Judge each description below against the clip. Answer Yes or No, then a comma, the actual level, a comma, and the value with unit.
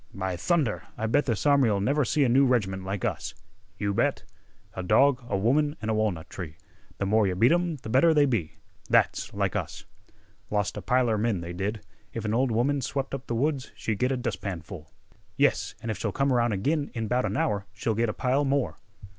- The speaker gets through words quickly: Yes, fast, 215 wpm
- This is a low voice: Yes, low, 115 Hz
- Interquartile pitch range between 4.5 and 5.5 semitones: Yes, average, 5.2 semitones